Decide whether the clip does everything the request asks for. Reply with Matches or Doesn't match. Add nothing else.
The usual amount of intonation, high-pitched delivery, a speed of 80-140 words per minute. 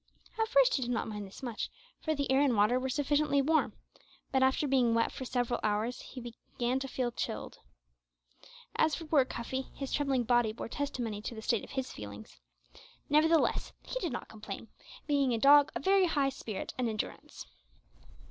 Doesn't match